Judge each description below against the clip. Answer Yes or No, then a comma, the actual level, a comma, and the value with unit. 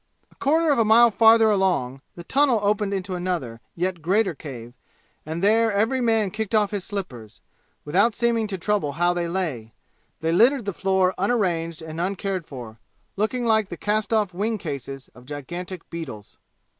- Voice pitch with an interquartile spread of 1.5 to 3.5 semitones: No, average, 5.0 semitones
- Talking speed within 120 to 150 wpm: No, average, 170 wpm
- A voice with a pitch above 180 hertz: Yes, high, 190 Hz